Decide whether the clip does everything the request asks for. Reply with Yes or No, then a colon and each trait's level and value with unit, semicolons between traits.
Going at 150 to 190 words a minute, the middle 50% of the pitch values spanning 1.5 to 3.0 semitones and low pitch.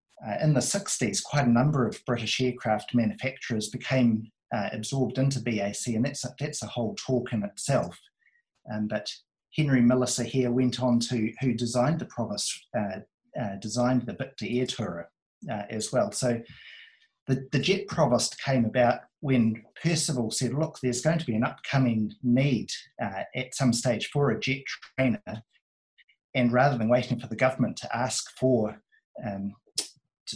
Yes: average, 165 wpm; average, 2.7 semitones; low, 125 Hz